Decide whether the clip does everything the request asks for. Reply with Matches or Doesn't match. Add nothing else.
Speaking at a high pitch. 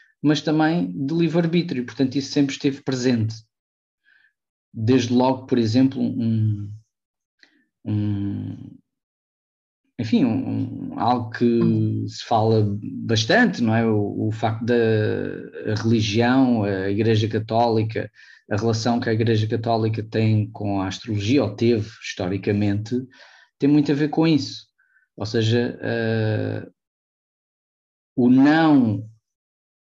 Doesn't match